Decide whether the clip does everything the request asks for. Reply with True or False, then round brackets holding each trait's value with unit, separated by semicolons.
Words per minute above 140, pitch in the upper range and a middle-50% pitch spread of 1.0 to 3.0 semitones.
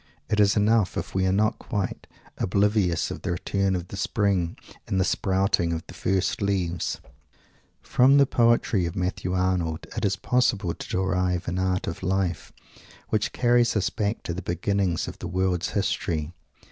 False (170 wpm; 95 Hz; 2.4 semitones)